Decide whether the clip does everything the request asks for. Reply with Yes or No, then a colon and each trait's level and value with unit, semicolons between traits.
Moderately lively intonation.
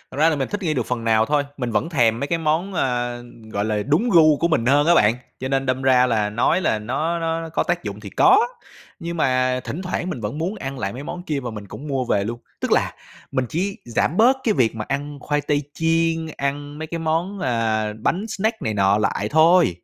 No: wide, 5.7 semitones